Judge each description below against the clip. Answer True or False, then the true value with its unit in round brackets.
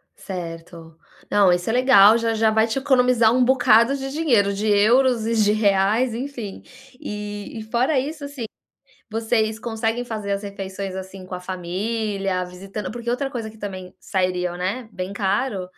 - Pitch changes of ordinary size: True (3.7 semitones)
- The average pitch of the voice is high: True (215 Hz)